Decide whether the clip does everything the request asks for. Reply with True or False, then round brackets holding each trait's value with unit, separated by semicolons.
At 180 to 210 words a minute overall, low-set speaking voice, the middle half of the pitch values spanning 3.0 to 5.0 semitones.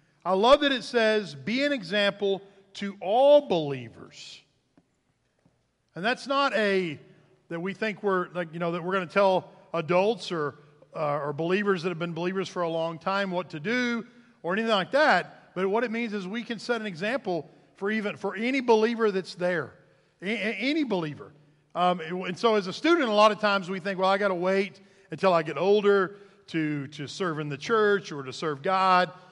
False (200 wpm; 190 Hz; 3.8 semitones)